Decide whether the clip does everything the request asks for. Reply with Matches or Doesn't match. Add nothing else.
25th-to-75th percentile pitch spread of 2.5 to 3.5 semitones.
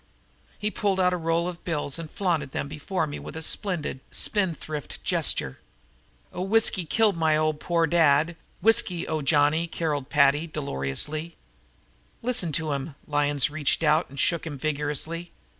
Matches